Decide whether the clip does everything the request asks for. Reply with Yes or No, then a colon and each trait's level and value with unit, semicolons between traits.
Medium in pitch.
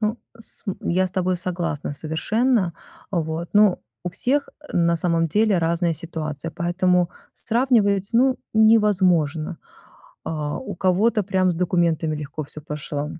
Yes: medium, 180 Hz